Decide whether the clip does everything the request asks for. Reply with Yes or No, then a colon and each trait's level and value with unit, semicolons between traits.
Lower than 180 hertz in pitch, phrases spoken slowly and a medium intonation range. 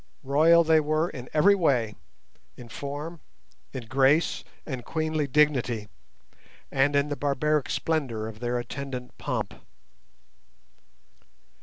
Yes: medium, 140 Hz; slow, 110 wpm; average, 3.8 semitones